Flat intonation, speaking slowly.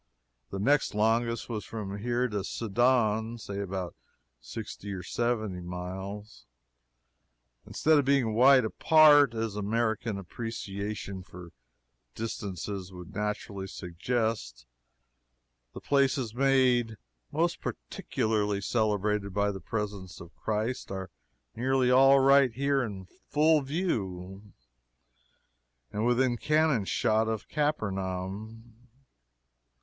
No: average, 4.2 semitones; slow, 105 wpm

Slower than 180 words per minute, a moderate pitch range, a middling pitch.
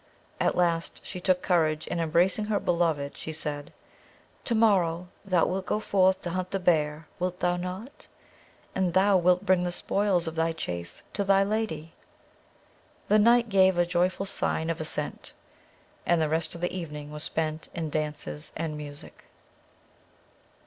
Yes: average, 165 wpm; average, 3.1 semitones; medium, 175 Hz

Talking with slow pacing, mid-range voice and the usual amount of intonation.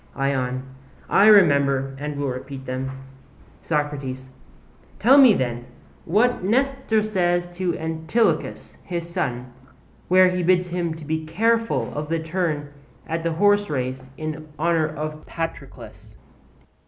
Yes: slow, 120 wpm; medium, 160 Hz; average, 4.7 semitones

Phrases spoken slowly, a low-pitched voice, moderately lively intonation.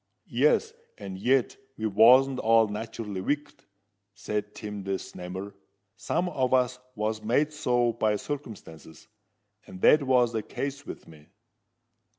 Yes: slow, 130 wpm; low, 115 Hz; average, 4.5 semitones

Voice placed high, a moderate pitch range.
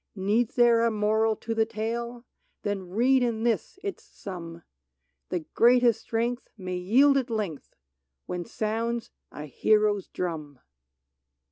Yes: high, 220 Hz; average, 3.9 semitones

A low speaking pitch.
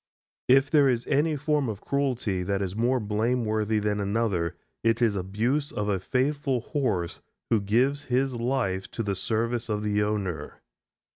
Yes: low, 115 Hz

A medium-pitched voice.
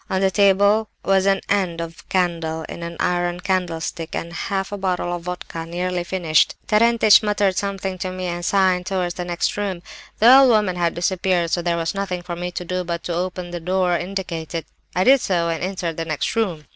Yes: medium, 180 Hz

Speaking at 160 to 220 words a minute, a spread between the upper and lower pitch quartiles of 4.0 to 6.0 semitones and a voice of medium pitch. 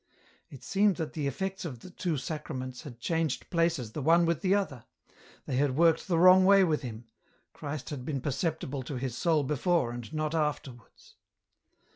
Yes: average, 180 wpm; average, 4.6 semitones; medium, 150 Hz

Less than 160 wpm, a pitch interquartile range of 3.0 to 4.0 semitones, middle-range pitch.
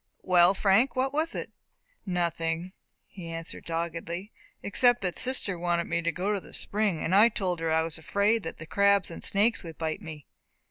No: average, 190 wpm; average, 3.5 semitones; medium, 180 Hz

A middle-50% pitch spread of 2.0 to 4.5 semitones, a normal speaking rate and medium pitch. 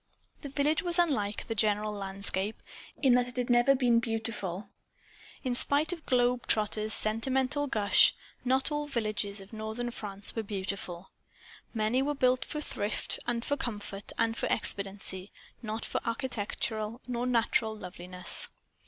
No: average, 3.7 semitones; average, 145 wpm; high, 225 Hz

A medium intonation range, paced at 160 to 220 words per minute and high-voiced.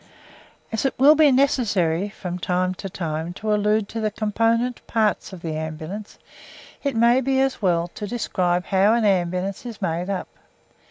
Yes: average, 4.4 semitones; average, 170 wpm; high, 205 Hz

